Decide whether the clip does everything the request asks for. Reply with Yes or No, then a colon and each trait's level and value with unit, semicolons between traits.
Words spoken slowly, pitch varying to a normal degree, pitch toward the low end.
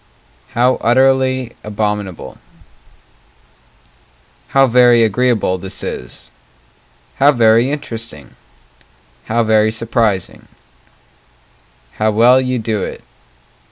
Yes: slow, 85 wpm; average, 3.0 semitones; low, 115 Hz